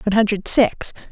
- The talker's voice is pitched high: Yes, high, 210 Hz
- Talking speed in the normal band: Yes, average, 160 wpm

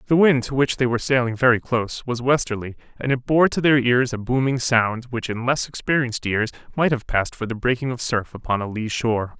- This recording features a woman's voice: No, male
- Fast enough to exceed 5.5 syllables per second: Yes, 5.9 syllables/s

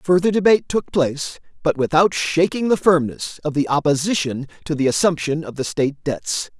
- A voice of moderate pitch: Yes, medium, 160 Hz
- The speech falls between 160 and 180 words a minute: Yes, average, 175 wpm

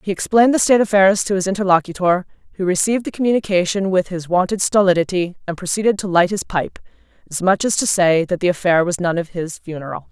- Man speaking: No, female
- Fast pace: Yes, fast, 215 wpm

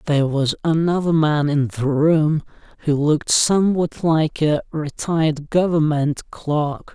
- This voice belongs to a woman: No, male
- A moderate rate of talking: No, slow, 130 wpm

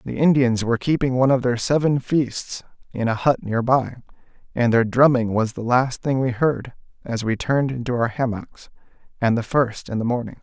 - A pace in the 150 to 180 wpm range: No, average, 200 wpm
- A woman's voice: No, male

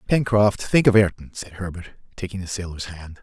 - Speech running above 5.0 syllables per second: Yes, 5.6 syllables/s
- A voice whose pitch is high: No, low, 100 Hz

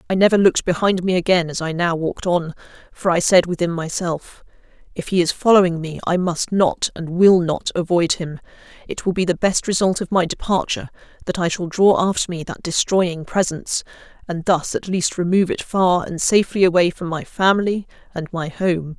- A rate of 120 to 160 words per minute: No, average, 195 wpm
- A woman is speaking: Yes, female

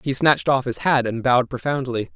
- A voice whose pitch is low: Yes, low, 130 Hz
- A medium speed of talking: No, fast, 225 wpm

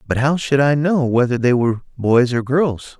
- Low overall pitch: Yes, low, 130 Hz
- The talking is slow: No, fast, 220 wpm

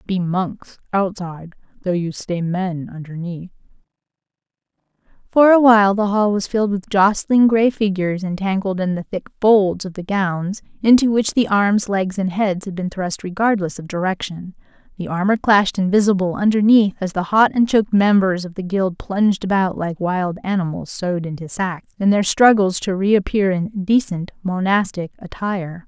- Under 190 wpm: Yes, average, 165 wpm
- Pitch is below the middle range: No, high, 190 Hz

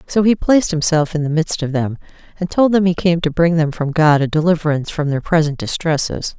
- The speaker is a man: No, female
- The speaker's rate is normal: No, fast, 235 wpm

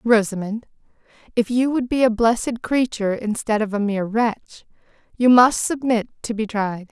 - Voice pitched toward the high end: Yes, high, 225 Hz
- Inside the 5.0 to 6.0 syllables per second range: Yes, 5.2 syllables/s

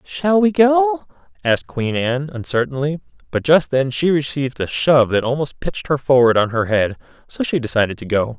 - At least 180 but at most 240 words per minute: Yes, average, 195 wpm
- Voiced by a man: Yes, male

